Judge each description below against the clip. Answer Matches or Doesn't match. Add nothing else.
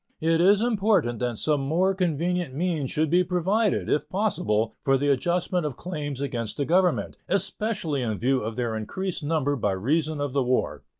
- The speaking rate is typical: Matches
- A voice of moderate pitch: Matches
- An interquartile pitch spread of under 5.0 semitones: Doesn't match